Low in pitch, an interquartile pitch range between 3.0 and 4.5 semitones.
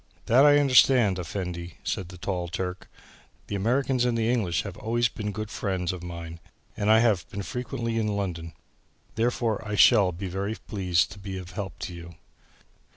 Yes: low, 100 Hz; average, 4.2 semitones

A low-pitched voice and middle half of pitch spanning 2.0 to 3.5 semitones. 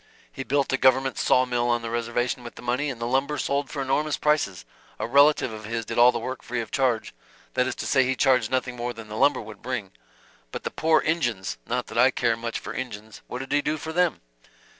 Yes: low, 125 Hz; average, 2.9 semitones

